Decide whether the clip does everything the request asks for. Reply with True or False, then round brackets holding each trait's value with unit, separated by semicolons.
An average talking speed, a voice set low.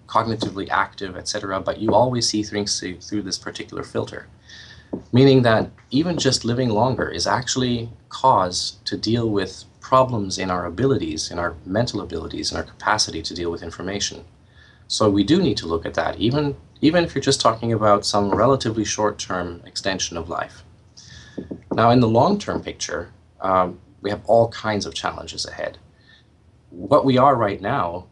True (170 wpm; 105 Hz)